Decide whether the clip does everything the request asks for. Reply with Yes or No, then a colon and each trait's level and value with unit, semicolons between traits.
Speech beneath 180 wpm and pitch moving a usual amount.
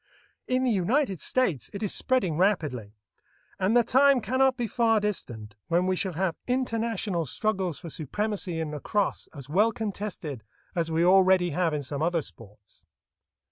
No: average, 160 wpm; wide, 5.7 semitones